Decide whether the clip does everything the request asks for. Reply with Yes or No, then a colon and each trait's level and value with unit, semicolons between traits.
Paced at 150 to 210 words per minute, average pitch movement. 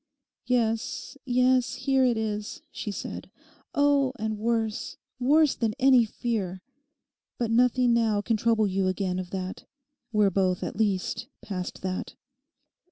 No: slow, 135 wpm; average, 3.9 semitones